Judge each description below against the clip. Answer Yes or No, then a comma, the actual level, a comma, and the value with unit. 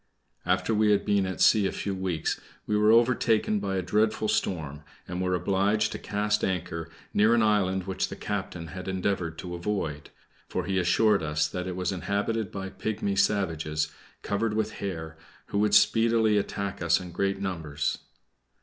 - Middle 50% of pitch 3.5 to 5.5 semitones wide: No, average, 2.8 semitones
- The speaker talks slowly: No, average, 175 wpm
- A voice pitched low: Yes, very low, 95 Hz